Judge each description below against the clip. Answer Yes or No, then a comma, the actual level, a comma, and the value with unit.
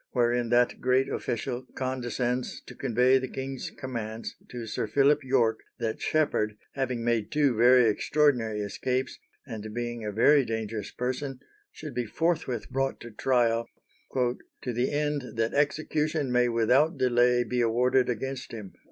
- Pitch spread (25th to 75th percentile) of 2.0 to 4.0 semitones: Yes, narrow, 2.5 semitones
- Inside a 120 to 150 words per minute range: Yes, average, 145 wpm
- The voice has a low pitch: Yes, low, 125 Hz